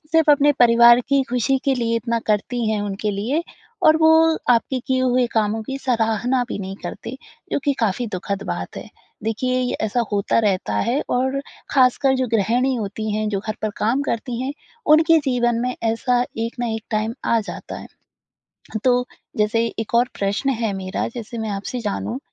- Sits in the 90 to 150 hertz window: No, high, 235 Hz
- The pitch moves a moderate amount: Yes, average, 3.2 semitones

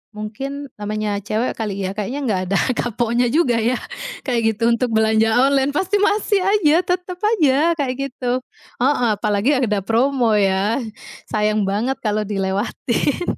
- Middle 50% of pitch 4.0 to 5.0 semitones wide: Yes, average, 4.6 semitones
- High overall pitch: Yes, high, 240 Hz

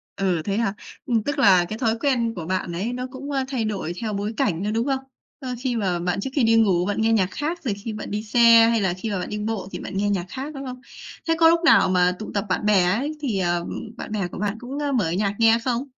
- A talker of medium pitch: No, high, 215 Hz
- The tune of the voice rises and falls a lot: No, average, 4.6 semitones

